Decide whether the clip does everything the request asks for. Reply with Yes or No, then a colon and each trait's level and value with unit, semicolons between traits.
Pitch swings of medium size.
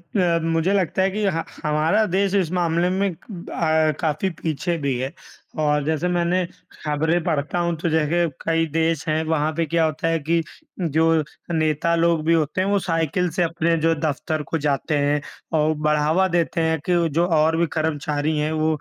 No: narrow, 2.0 semitones